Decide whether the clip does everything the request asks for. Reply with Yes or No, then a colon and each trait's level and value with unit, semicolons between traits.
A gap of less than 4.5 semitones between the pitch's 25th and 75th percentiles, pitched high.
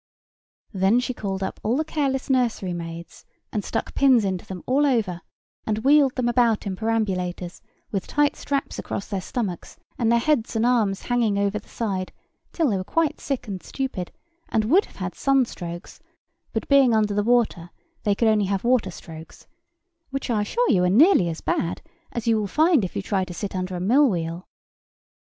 No: average, 5.2 semitones; high, 215 Hz